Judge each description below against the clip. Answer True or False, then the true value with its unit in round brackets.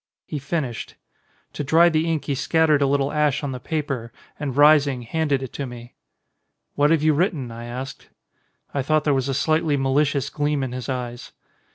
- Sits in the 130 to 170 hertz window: True (140 Hz)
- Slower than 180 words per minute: False (190 wpm)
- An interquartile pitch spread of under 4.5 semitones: True (2.7 semitones)